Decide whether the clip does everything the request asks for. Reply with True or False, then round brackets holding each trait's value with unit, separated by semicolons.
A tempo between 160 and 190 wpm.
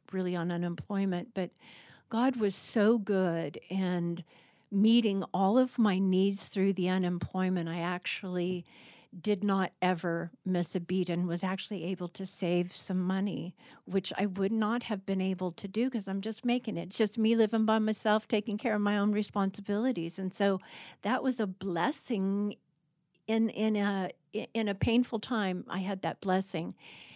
True (170 wpm)